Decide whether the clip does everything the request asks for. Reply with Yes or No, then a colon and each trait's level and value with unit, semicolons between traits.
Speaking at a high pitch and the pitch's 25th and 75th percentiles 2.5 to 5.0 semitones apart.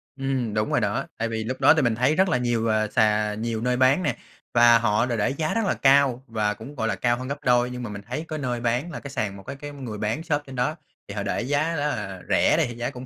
No: low, 125 Hz; average, 4.0 semitones